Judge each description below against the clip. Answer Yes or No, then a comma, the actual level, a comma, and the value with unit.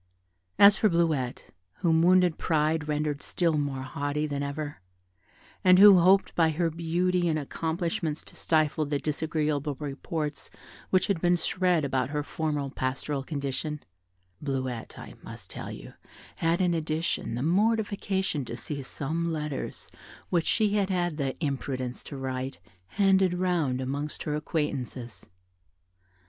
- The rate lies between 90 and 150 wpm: Yes, average, 140 wpm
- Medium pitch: Yes, medium, 155 Hz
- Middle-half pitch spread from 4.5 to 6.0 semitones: No, average, 3.6 semitones